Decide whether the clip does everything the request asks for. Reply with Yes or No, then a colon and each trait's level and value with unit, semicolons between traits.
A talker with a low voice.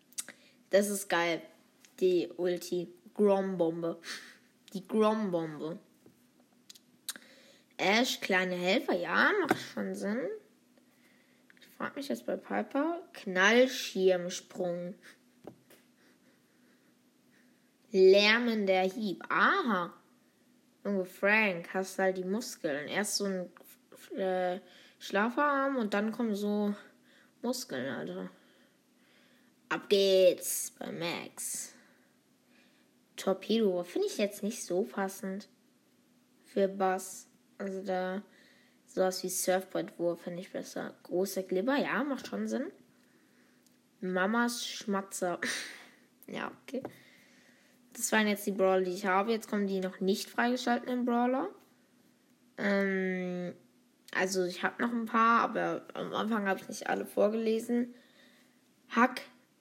No: high, 205 Hz